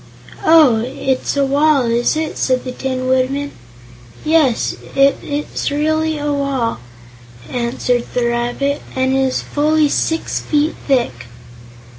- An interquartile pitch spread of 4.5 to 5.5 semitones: No, average, 2.9 semitones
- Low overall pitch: No, very high, 275 Hz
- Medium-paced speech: No, slow, 130 wpm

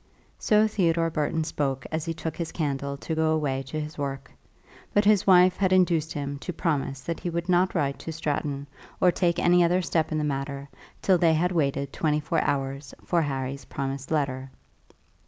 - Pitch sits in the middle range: Yes, medium, 155 Hz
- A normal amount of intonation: Yes, average, 3.6 semitones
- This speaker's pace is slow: No, average, 190 wpm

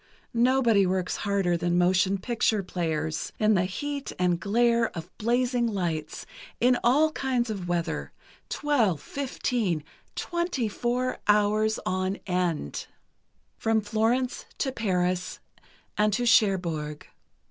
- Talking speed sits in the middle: No, slow, 110 wpm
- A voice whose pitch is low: No, high, 210 Hz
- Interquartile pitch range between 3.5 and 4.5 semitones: No, average, 5.1 semitones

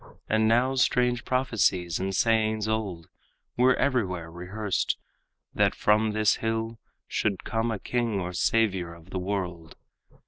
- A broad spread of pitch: No, average, 3.7 semitones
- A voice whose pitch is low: Yes, low, 110 Hz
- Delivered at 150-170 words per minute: No, slow, 135 wpm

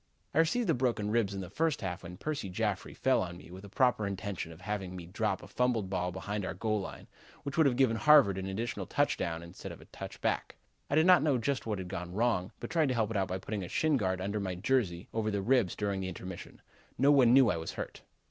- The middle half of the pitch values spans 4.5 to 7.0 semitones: Yes, average, 5.2 semitones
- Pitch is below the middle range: Yes, low, 105 Hz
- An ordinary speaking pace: No, fast, 250 wpm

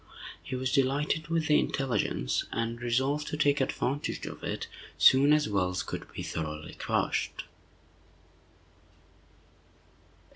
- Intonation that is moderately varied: Yes, average, 4.2 semitones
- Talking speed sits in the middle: No, slow, 115 wpm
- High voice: No, low, 135 Hz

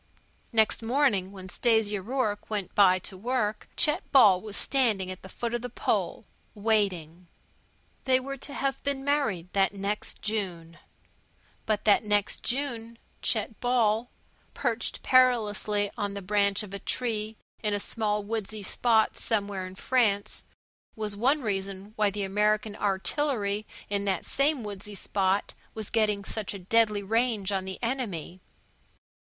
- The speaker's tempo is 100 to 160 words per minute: Yes, average, 150 wpm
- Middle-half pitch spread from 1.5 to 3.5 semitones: Yes, average, 2.8 semitones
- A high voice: Yes, high, 210 Hz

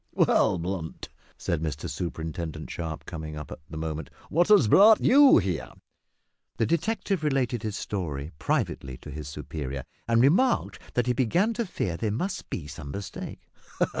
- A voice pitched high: No, very low, 95 Hz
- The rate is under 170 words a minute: Yes, average, 160 wpm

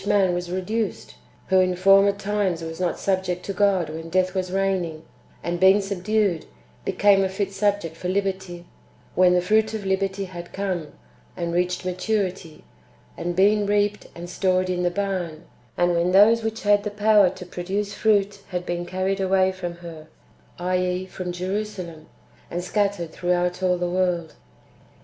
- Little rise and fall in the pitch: Yes, narrow, 2.1 semitones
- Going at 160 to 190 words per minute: Yes, average, 165 wpm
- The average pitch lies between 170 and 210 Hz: Yes, medium, 185 Hz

